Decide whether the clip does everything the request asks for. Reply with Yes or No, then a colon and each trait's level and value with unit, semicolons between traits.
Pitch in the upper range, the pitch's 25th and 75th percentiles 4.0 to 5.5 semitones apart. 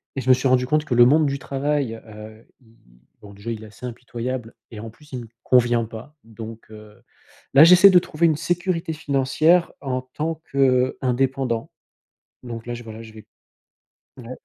No: low, 125 Hz; average, 4.3 semitones